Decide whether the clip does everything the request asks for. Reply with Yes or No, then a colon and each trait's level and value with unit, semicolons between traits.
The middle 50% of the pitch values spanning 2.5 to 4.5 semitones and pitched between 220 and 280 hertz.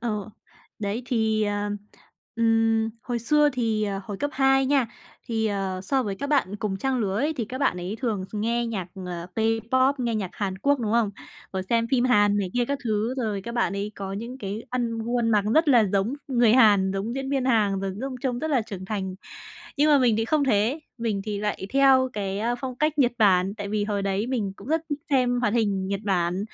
Yes: average, 3.9 semitones; high, 225 Hz